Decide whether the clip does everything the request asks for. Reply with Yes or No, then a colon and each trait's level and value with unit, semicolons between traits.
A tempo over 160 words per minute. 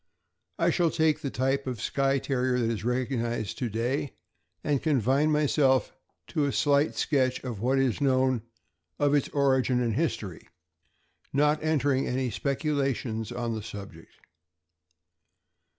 No: average, 140 wpm